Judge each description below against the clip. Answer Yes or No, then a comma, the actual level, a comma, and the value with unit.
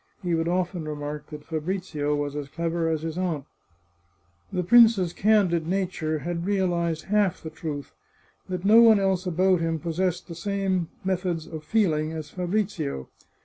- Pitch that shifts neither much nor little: Yes, average, 3.1 semitones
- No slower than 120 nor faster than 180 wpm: Yes, average, 160 wpm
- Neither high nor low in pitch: Yes, medium, 170 Hz